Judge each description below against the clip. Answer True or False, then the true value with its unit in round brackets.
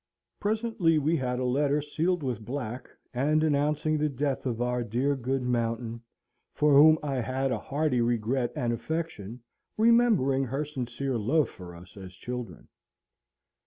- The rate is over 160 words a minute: False (150 wpm)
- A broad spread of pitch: False (3.9 semitones)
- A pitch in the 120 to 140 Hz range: True (135 Hz)